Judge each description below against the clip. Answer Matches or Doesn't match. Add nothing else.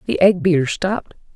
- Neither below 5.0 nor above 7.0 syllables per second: Matches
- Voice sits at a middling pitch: Matches